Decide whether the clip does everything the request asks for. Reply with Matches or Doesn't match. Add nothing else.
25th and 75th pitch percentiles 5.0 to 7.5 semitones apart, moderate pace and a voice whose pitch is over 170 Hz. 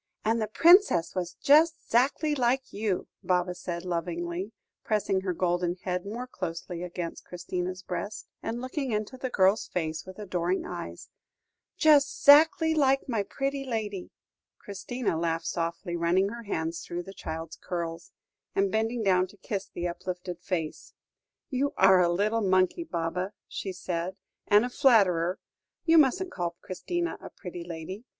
Matches